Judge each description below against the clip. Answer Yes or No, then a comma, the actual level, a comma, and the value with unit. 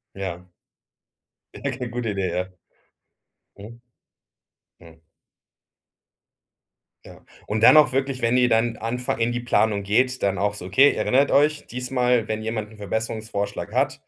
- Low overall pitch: Yes, low, 115 Hz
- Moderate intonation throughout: Yes, average, 3.4 semitones